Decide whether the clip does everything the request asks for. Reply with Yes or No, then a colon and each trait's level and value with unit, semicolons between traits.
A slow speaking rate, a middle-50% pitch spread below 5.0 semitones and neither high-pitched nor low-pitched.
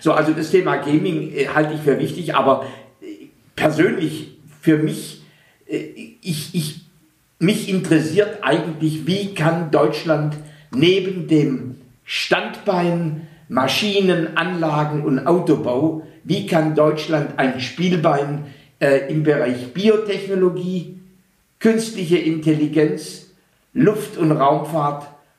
Yes: slow, 105 wpm; average, 3.3 semitones; medium, 160 Hz